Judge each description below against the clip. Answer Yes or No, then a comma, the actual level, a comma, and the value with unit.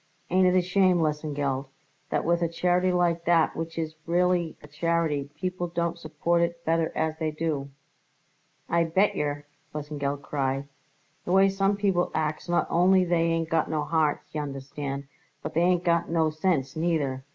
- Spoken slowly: No, average, 170 wpm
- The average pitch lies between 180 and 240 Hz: No, medium, 165 Hz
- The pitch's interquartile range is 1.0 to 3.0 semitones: Yes, average, 2.7 semitones